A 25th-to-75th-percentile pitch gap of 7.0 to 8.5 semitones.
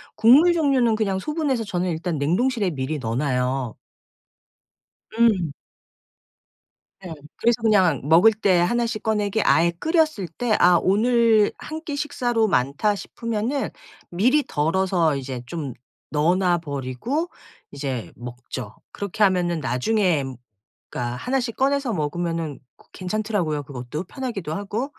Yes: wide, 7.5 semitones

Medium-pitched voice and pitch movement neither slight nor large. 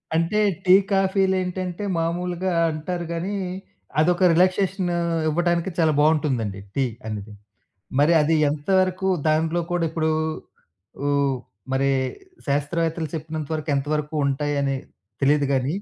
Yes: medium, 160 Hz; average, 3.5 semitones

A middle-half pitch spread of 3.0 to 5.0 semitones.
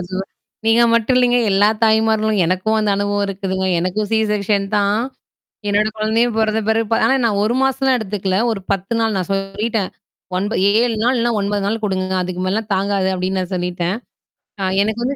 No: narrow, 2.4 semitones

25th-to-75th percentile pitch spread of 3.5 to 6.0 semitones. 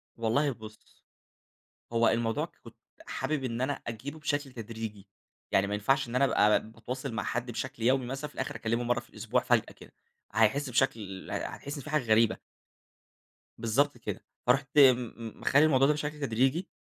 Yes: average, 3.8 semitones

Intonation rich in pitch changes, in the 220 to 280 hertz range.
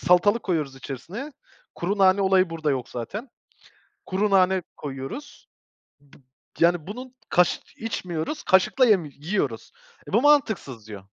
No: wide, 6.2 semitones; medium, 185 Hz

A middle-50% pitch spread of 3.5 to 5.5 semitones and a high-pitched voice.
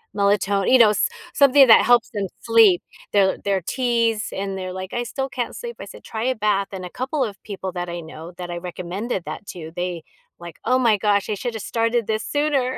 Yes: average, 4.4 semitones; high, 210 Hz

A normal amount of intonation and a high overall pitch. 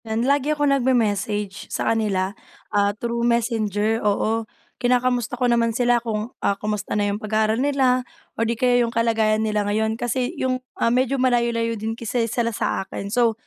No: narrow, 2.3 semitones; high, 230 Hz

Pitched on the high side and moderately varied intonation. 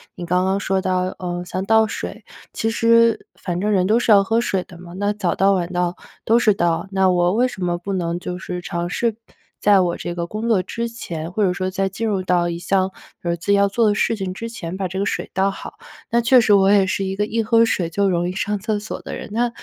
Yes: high, 195 Hz; average, 3.0 semitones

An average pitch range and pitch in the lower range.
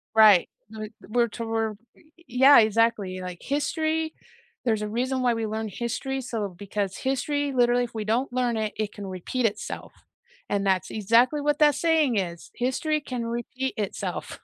No: average, 3.8 semitones; high, 235 Hz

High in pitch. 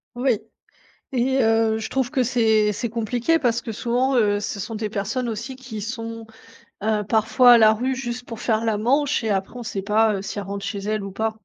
Yes: high, 225 Hz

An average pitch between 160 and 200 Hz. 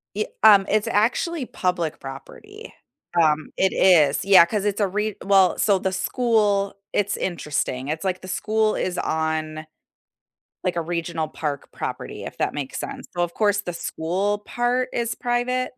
Yes: high, 190 Hz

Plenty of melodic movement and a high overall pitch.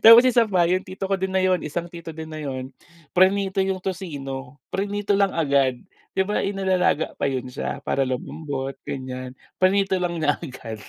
No: wide, 5.9 semitones; medium, 170 Hz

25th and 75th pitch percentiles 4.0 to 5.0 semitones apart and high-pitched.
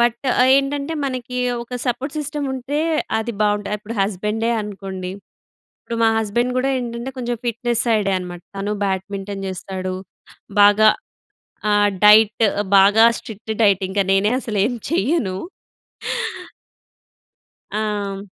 No: average, 3.3 semitones; high, 215 Hz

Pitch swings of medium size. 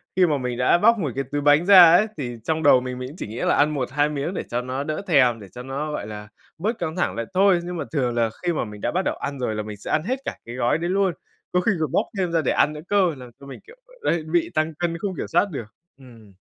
No: wide, 5.7 semitones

